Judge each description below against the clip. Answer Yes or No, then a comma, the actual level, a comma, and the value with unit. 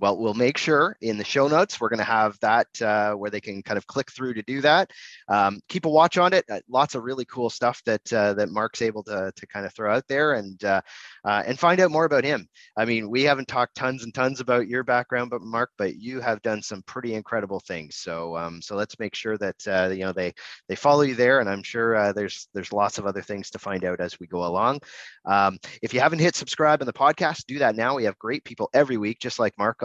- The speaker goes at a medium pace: No, fast, 265 wpm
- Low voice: Yes, low, 110 Hz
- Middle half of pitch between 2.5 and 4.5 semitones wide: Yes, average, 4.2 semitones